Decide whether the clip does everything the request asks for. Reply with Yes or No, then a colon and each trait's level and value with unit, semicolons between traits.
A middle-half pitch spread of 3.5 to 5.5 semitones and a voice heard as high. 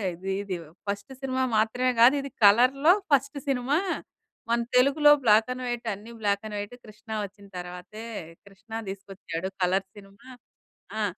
Yes: average, 4.1 semitones; high, 220 Hz